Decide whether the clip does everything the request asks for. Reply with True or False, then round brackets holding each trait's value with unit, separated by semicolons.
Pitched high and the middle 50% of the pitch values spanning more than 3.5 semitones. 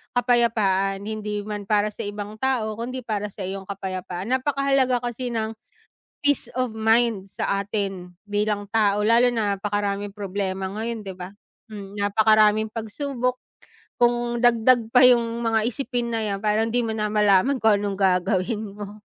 False (215 Hz; 2.9 semitones)